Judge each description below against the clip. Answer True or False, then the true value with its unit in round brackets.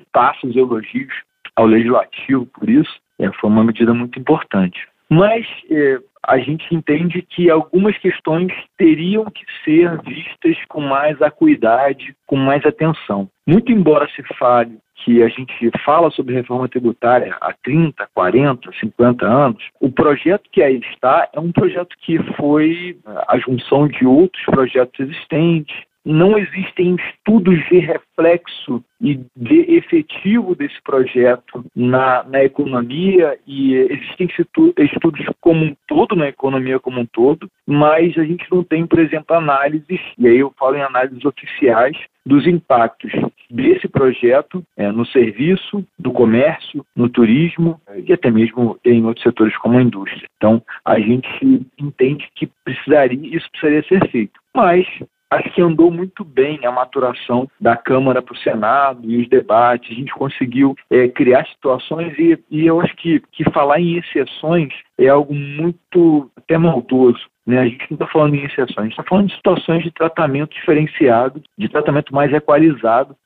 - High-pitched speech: False (150 Hz)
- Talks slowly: False (155 wpm)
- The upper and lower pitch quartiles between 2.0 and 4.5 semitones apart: False (5.3 semitones)